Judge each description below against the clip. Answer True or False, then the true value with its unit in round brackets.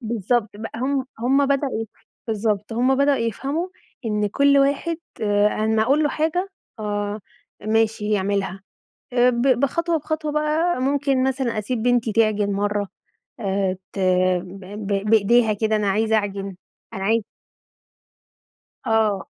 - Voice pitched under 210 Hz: False (225 Hz)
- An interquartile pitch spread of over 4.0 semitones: True (4.8 semitones)